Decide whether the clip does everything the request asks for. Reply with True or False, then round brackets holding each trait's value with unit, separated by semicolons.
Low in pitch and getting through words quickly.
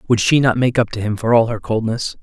True (115 Hz; 295 wpm)